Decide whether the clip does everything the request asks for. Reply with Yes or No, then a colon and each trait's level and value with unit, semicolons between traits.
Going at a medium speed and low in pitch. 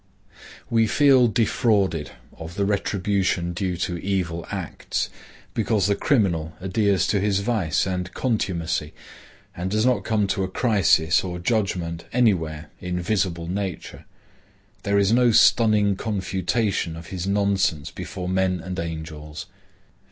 No: slow, 130 wpm; very low, 95 Hz